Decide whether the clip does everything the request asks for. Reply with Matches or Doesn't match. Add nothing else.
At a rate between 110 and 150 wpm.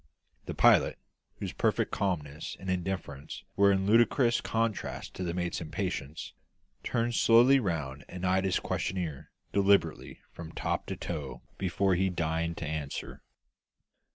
Matches